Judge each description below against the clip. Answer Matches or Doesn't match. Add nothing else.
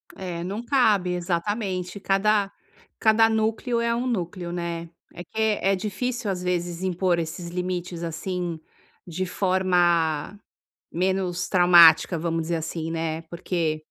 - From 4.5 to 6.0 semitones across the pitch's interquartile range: Doesn't match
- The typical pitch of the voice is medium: Matches